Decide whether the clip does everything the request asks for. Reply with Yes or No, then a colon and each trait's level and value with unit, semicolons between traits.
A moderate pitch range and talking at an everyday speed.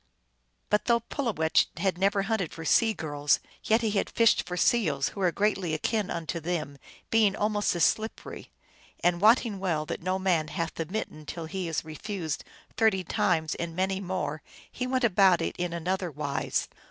Yes: average, 4.4 semitones; average, 175 wpm